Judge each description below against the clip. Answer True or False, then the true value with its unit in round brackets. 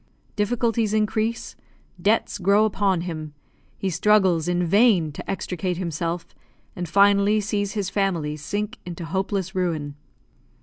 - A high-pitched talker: True (195 Hz)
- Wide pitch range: False (3.5 semitones)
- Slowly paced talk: True (125 wpm)